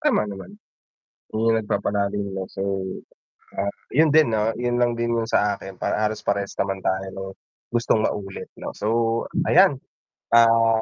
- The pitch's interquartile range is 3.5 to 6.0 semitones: No, average, 2.9 semitones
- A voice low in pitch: Yes, low, 110 Hz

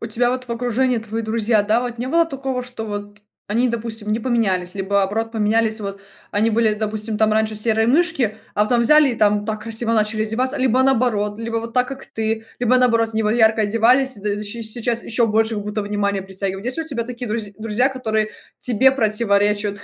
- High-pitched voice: Yes, high, 225 Hz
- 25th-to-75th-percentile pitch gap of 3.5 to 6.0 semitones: No, narrow, 2.5 semitones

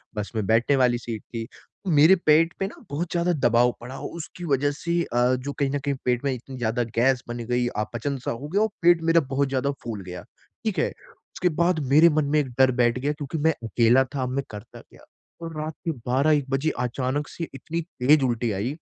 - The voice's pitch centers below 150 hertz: Yes, low, 135 Hz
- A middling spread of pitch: Yes, average, 4.2 semitones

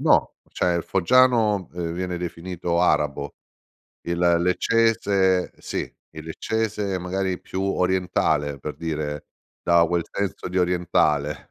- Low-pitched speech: Yes, very low, 90 Hz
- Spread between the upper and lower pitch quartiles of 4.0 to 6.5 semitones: No, narrow, 2.6 semitones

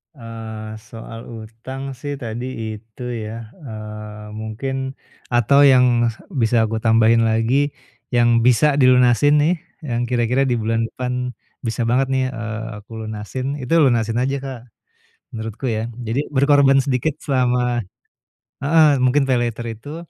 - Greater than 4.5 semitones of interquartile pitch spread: No, average, 2.9 semitones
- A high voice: No, low, 120 Hz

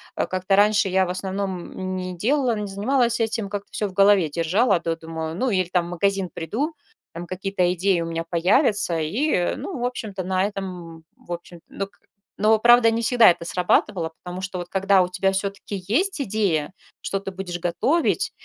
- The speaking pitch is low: No, high, 190 Hz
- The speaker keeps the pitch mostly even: No, average, 3.1 semitones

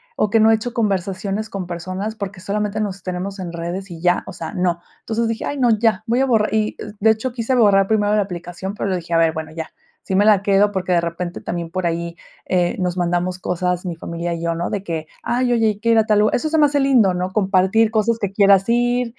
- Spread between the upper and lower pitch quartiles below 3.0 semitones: No, average, 3.7 semitones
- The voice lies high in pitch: Yes, high, 195 Hz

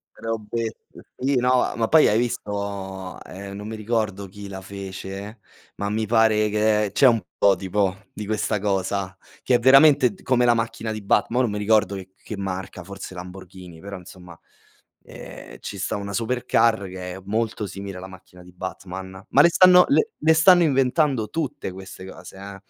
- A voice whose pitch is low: Yes, low, 100 Hz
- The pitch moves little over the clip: No, average, 3.4 semitones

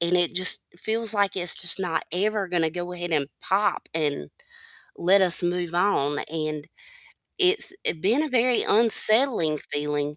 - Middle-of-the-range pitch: Yes, medium, 180 Hz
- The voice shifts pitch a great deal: No, average, 4.6 semitones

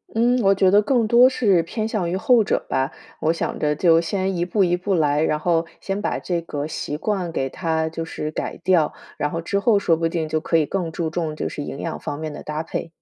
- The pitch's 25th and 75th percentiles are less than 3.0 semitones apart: No, average, 3.7 semitones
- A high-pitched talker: No, medium, 170 Hz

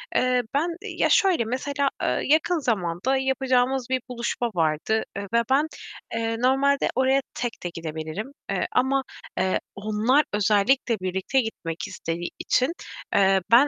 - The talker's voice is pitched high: Yes, high, 245 Hz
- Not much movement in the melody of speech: No, average, 5.3 semitones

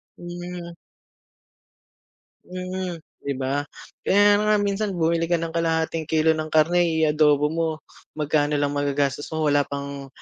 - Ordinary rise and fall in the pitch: Yes, average, 3.1 semitones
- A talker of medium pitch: Yes, medium, 160 Hz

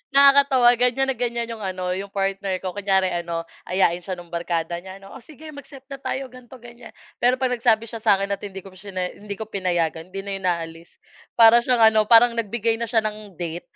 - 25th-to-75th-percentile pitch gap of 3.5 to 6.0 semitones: Yes, average, 4.5 semitones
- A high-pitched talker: Yes, high, 205 Hz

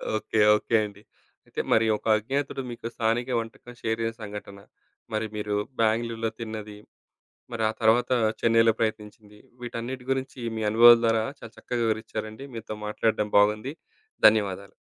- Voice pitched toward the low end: Yes, low, 110 Hz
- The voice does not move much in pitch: Yes, narrow, 1.5 semitones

